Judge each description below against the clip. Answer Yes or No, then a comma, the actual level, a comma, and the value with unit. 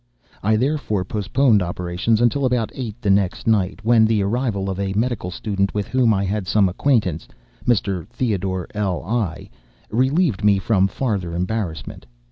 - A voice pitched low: Yes, low, 105 Hz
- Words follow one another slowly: No, average, 150 wpm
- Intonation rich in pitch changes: No, average, 3.5 semitones